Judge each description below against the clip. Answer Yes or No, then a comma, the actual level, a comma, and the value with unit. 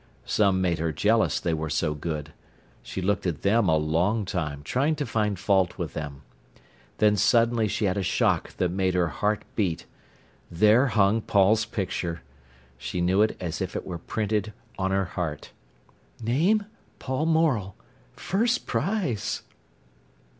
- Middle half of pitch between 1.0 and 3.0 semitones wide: No, average, 4.5 semitones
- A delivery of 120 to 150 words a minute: Yes, average, 145 wpm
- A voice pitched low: Yes, low, 100 Hz